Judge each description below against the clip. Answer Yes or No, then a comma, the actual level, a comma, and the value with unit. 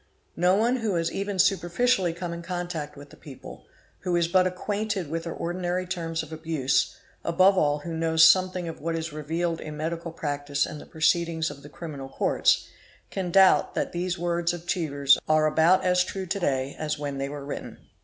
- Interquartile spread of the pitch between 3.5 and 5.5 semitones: No, average, 2.9 semitones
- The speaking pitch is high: No, medium, 170 Hz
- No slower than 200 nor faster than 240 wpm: Yes, fast, 205 wpm